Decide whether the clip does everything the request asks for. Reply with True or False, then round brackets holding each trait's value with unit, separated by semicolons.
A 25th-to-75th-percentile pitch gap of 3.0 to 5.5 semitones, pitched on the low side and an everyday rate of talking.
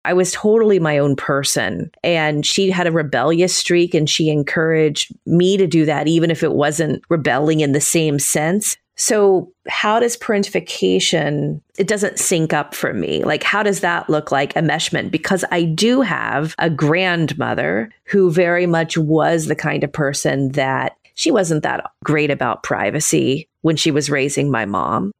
False (3.5 semitones; 160 Hz; 175 wpm)